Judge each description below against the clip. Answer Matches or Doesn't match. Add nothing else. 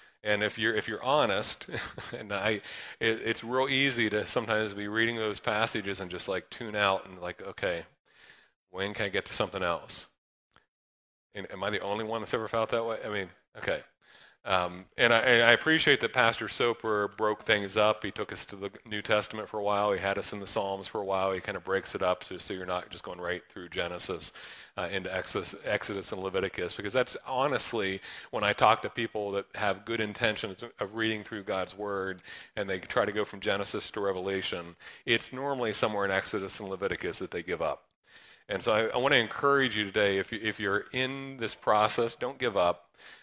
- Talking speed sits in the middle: Doesn't match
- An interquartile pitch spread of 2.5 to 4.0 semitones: Matches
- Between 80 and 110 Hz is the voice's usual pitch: Matches